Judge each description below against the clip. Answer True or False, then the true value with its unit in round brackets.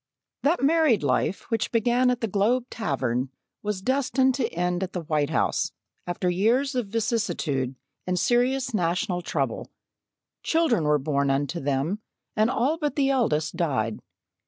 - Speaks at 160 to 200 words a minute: False (150 wpm)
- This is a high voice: True (205 Hz)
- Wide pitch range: True (8.4 semitones)